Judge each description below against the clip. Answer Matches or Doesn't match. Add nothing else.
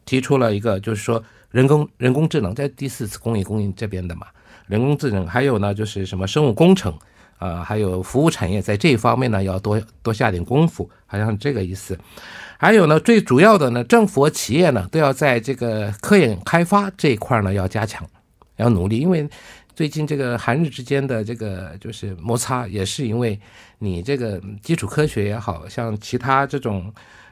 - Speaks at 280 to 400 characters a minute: Matches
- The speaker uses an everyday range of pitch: Doesn't match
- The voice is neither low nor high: Doesn't match